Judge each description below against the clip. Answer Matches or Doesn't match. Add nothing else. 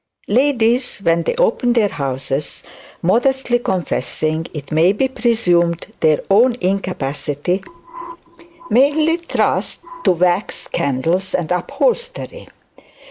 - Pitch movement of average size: Doesn't match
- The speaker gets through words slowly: Matches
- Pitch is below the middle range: Doesn't match